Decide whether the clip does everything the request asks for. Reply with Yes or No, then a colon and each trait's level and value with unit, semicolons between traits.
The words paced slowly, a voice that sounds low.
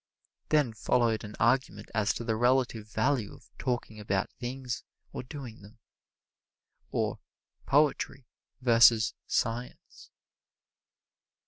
Yes: slow, 105 wpm; low, 120 Hz